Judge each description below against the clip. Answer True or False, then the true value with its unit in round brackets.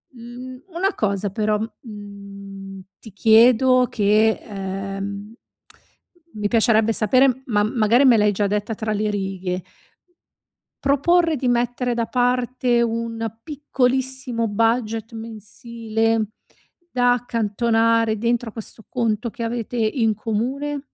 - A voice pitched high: True (225 Hz)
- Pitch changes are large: False (2.8 semitones)